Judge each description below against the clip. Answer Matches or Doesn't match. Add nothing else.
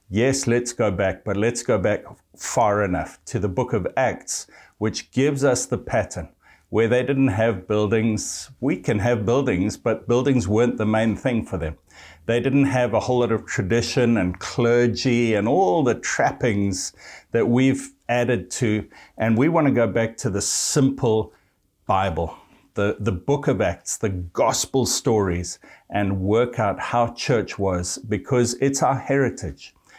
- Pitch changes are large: Doesn't match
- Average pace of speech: Matches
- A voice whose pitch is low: Matches